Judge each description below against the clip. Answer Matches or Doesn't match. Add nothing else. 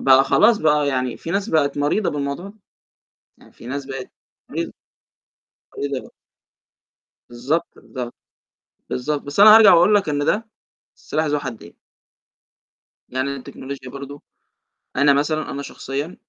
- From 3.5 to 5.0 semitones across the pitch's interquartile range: Doesn't match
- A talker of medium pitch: Matches